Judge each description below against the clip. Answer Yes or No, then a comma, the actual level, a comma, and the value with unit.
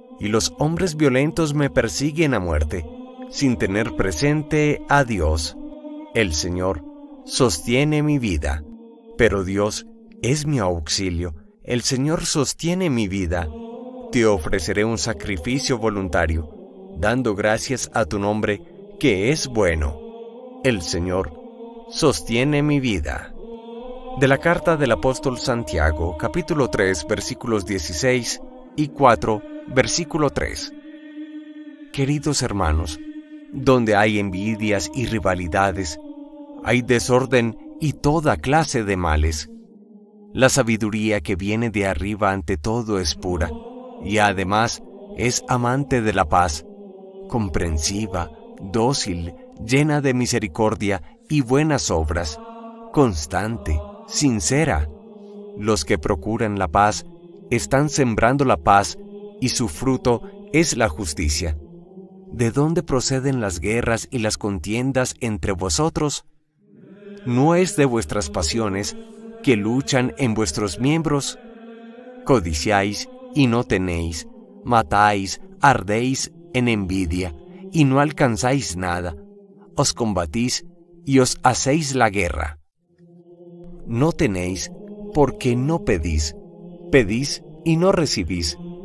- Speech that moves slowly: Yes, slow, 110 wpm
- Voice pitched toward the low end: Yes, low, 130 Hz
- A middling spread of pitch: No, wide, 9.0 semitones